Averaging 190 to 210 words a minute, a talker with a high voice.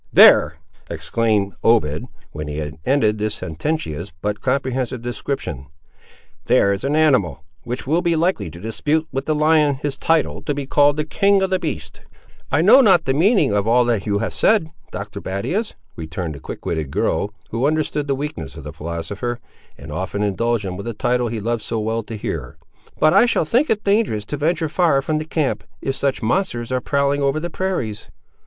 No: average, 195 wpm; low, 125 Hz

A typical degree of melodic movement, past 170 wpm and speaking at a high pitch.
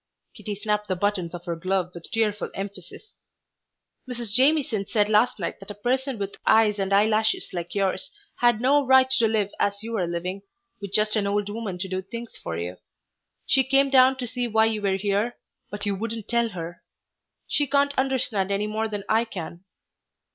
Yes: average, 3.3 semitones; average, 190 wpm; high, 210 Hz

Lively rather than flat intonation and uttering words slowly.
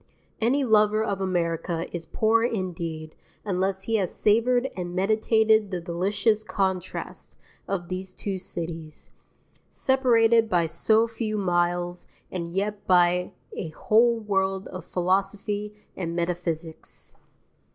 No: average, 3.7 semitones; slow, 120 wpm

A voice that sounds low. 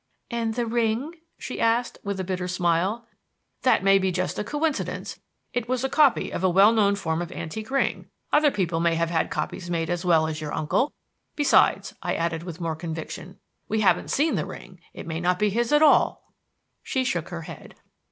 No: high, 195 Hz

